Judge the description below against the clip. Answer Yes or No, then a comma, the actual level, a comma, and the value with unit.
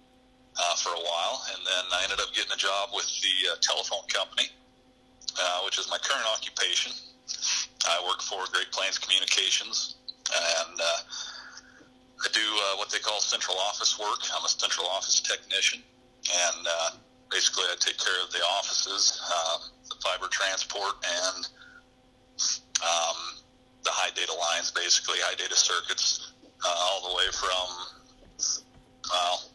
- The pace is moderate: Yes, average, 150 wpm